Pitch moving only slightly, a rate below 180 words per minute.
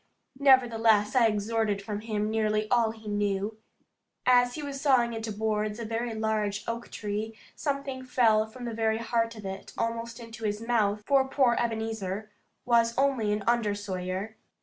Yes: narrow, 2.1 semitones; average, 160 wpm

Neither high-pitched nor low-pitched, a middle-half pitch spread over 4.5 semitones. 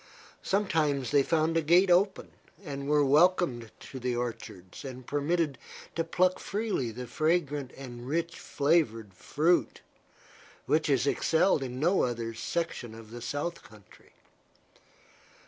Yes: medium, 145 Hz; wide, 5.4 semitones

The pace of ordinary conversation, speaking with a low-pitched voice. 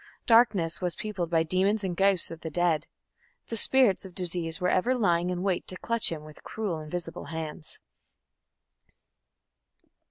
No: average, 155 wpm; medium, 180 Hz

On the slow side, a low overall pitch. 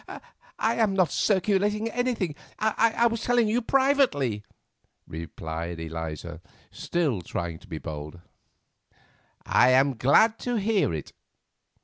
No: slow, 115 wpm; medium, 175 Hz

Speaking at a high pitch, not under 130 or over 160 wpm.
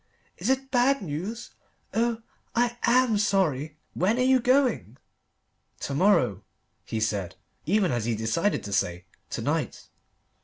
Yes: high, 195 Hz; average, 140 wpm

